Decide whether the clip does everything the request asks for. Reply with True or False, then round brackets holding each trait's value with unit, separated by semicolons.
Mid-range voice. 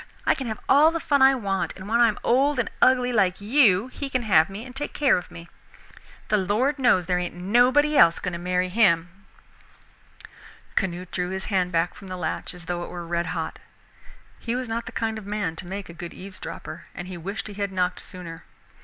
False (195 Hz)